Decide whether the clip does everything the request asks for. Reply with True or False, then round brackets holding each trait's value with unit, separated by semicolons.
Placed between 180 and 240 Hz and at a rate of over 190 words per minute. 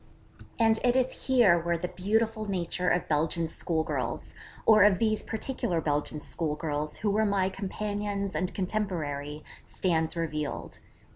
False (185 Hz; 135 wpm)